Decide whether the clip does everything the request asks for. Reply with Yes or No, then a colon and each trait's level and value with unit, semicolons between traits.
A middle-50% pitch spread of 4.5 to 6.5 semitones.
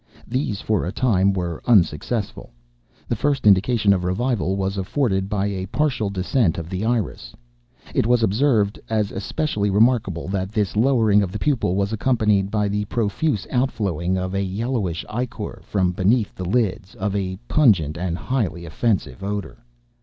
No: average, 3.7 semitones